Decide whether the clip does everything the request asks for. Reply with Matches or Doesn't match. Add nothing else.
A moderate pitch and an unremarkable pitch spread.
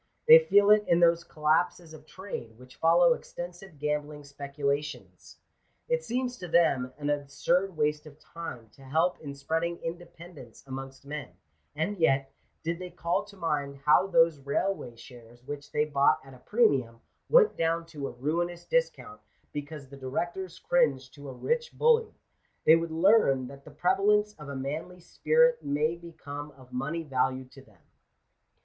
Matches